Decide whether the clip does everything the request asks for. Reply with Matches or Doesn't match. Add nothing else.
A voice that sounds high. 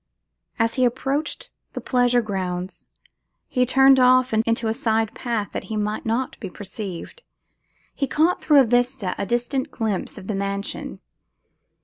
Matches